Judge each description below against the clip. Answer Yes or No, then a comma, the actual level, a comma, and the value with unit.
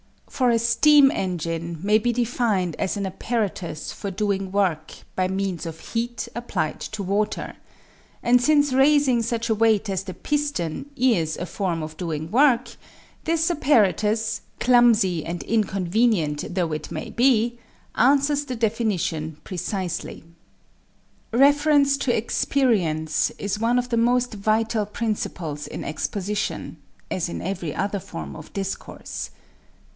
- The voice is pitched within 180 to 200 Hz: No, high, 215 Hz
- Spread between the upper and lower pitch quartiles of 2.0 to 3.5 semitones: No, average, 5.0 semitones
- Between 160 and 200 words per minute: No, slow, 135 wpm